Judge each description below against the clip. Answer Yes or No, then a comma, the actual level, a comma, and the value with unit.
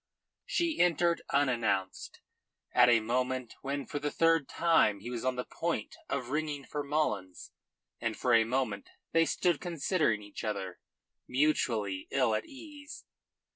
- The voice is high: No, low, 130 Hz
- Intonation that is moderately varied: No, wide, 5.8 semitones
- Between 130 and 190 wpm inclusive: Yes, average, 145 wpm